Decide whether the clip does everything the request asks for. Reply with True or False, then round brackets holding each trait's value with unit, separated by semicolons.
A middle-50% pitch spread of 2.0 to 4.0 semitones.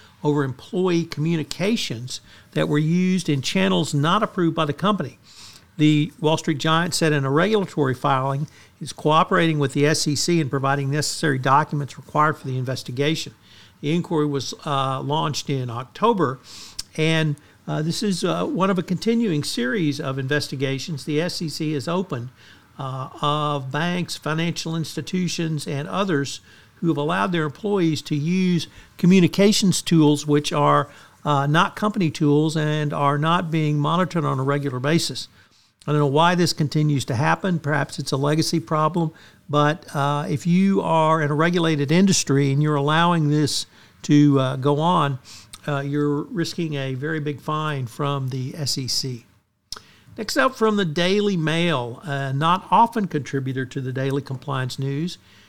True (3.2 semitones)